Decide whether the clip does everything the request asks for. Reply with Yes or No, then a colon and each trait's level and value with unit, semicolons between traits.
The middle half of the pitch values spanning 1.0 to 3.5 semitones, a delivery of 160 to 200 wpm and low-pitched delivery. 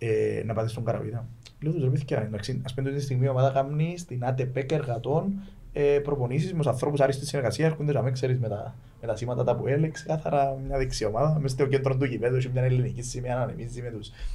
No: average, 3.0 semitones; fast, 220 wpm; low, 130 Hz